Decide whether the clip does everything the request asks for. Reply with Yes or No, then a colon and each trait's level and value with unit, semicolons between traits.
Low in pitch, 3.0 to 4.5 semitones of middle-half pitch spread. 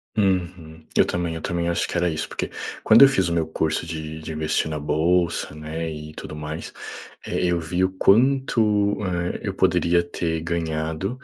No: very low, 85 Hz; narrow, 2.6 semitones